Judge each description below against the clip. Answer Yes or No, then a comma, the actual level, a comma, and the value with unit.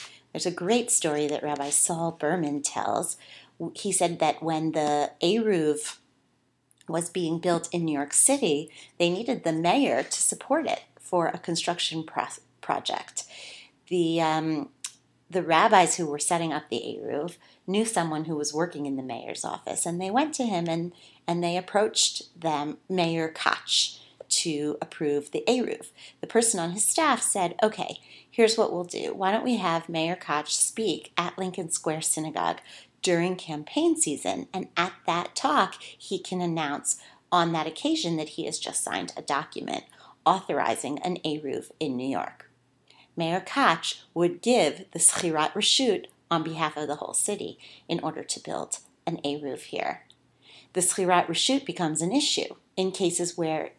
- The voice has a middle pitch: Yes, medium, 170 Hz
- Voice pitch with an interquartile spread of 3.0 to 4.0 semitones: Yes, average, 3.3 semitones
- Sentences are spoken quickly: No, average, 165 wpm